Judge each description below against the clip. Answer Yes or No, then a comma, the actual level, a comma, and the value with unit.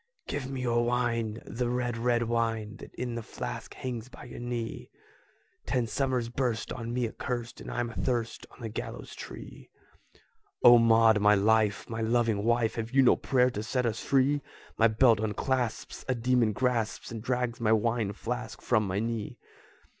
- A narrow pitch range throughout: Yes, narrow, 1.8 semitones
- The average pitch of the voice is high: No, low, 115 Hz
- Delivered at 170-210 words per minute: Yes, average, 175 wpm